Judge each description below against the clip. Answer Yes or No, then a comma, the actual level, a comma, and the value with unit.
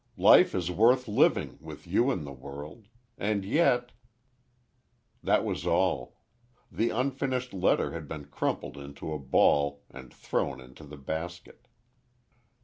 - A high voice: No, very low, 85 Hz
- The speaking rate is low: Yes, slow, 130 wpm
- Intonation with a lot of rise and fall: Yes, wide, 8.8 semitones